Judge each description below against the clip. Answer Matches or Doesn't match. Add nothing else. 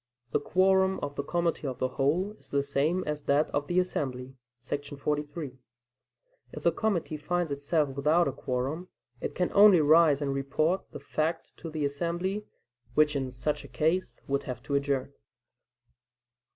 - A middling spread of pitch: Matches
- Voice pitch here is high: Doesn't match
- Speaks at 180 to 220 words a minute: Doesn't match